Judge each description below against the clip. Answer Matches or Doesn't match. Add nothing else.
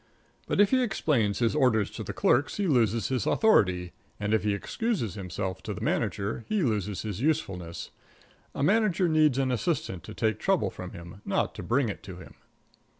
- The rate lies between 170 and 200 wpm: Matches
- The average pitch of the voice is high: Doesn't match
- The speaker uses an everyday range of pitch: Doesn't match